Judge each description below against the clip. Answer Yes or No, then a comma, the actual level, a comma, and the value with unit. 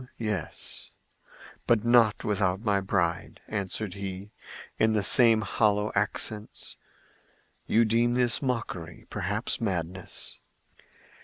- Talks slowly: Yes, slow, 95 wpm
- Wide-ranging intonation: No, average, 2.9 semitones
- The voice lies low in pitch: Yes, low, 105 Hz